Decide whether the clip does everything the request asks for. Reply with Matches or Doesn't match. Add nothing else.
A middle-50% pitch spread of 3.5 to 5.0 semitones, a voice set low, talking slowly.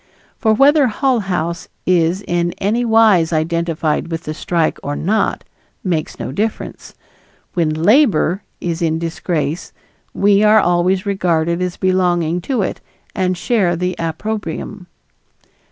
Doesn't match